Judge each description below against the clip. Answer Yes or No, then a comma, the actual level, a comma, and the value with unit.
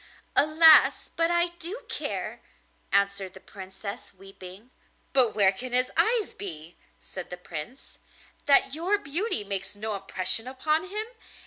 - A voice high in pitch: Yes, high, 225 Hz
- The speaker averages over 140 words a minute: No, slow, 135 wpm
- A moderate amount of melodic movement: No, wide, 8.7 semitones